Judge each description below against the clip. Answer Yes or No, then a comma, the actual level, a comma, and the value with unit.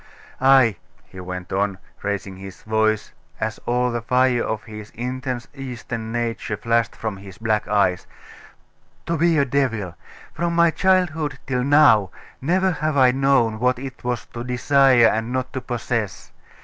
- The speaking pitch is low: Yes, low, 120 Hz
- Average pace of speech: Yes, average, 155 wpm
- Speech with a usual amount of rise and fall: Yes, average, 3.9 semitones